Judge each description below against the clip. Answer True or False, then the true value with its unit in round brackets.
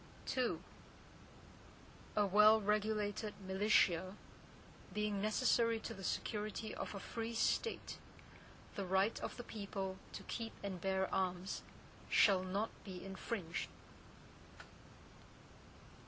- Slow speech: True (105 wpm)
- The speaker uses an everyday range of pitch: False (2.3 semitones)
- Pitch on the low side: False (205 Hz)